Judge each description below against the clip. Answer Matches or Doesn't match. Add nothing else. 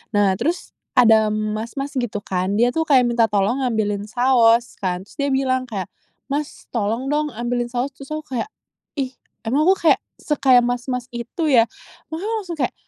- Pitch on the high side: Matches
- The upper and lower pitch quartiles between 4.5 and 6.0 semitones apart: Doesn't match